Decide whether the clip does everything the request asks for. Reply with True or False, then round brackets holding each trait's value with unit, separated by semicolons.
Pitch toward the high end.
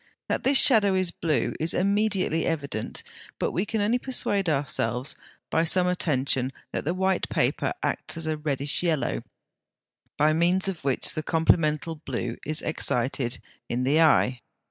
False (160 Hz)